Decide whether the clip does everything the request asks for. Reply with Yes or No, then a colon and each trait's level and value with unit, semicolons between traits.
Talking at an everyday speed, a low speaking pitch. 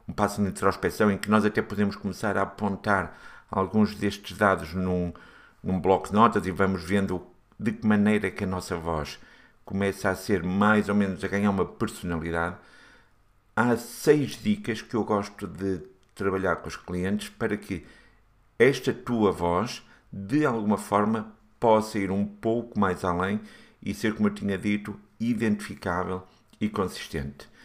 Yes: average, 165 wpm; low, 100 Hz